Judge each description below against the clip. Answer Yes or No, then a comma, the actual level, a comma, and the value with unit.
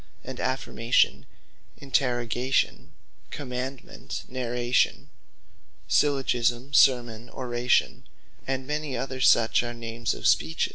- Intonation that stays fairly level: Yes, narrow, 1.8 semitones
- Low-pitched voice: Yes, low, 125 Hz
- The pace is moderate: No, slow, 90 wpm